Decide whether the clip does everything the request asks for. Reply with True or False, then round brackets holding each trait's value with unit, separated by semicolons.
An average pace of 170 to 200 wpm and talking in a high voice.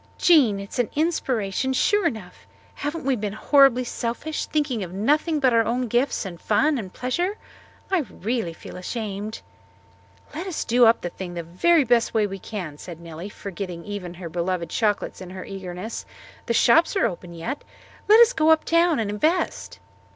True (180 wpm; 225 Hz)